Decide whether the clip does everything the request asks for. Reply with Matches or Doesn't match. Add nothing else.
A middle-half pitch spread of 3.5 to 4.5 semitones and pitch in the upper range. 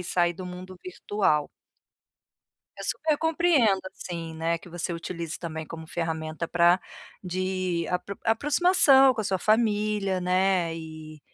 Doesn't match